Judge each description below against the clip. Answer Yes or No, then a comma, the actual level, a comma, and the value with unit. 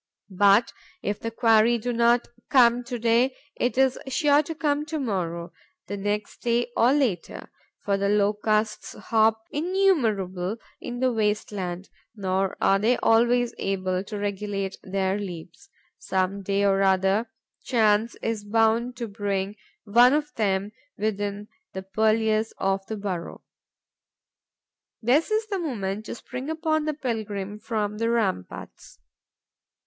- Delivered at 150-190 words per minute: No, average, 140 wpm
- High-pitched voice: Yes, high, 215 Hz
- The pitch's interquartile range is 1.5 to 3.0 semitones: No, average, 3.6 semitones